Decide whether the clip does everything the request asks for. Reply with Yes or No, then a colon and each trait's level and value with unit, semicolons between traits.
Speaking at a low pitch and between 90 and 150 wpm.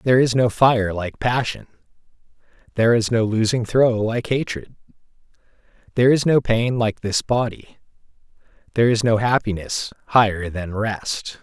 Yes: low, 115 Hz; average, 140 wpm